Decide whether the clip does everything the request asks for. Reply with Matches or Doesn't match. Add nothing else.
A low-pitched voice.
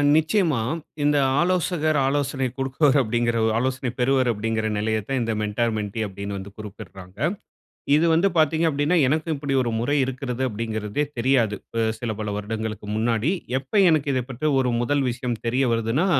Matches